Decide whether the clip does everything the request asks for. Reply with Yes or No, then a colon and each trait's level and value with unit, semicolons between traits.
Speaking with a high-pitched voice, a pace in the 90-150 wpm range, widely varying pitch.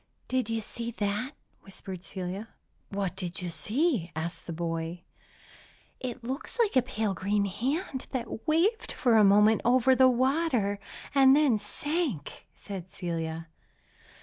Yes: high, 215 Hz; slow, 135 wpm; wide, 5.8 semitones